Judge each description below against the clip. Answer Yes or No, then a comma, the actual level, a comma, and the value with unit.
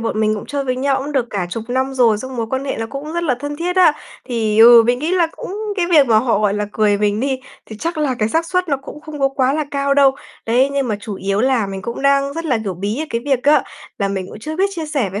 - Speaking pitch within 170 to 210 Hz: No, very high, 260 Hz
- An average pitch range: Yes, average, 4.9 semitones